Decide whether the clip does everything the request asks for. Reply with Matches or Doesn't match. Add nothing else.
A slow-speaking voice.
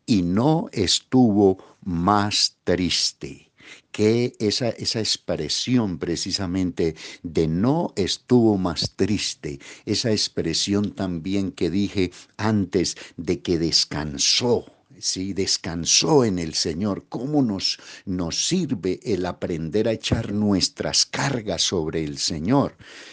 Matches